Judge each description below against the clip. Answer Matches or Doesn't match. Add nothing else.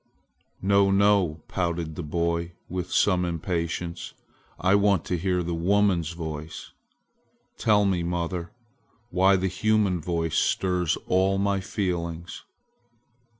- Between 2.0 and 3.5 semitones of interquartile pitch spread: Matches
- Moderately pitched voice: Doesn't match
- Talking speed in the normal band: Doesn't match